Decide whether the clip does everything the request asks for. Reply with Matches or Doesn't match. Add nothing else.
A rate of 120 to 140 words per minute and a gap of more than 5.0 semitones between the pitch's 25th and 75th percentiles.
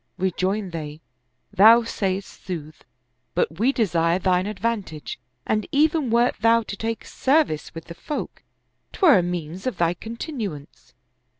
Matches